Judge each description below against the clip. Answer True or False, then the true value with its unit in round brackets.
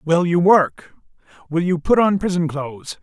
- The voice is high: False (170 Hz)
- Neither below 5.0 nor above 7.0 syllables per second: False (4.6 syllables/s)